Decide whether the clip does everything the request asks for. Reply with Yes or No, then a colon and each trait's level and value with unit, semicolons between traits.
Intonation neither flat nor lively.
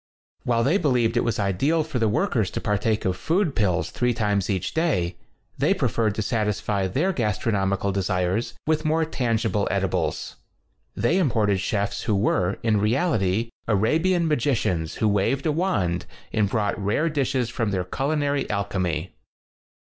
No: wide, 6.0 semitones